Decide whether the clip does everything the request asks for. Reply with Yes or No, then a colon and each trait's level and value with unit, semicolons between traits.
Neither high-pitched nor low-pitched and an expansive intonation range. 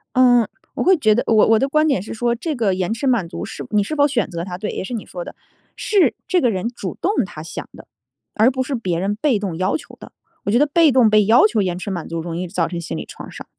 No: high, 220 Hz; wide, 5.7 semitones